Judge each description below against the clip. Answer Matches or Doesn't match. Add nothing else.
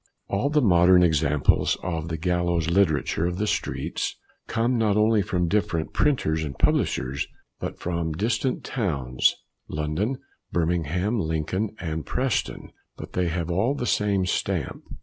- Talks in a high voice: Doesn't match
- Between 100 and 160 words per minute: Matches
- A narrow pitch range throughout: Doesn't match